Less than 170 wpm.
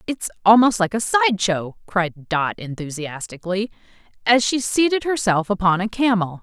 Yes: average, 150 wpm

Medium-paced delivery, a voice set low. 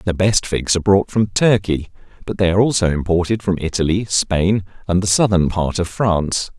Yes: average, 190 wpm; very low, 95 Hz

